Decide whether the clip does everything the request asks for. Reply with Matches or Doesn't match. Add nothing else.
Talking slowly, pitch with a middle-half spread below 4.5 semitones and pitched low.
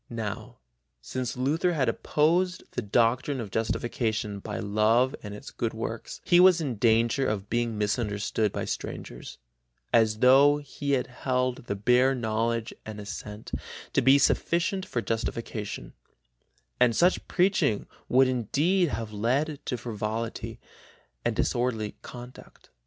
Matches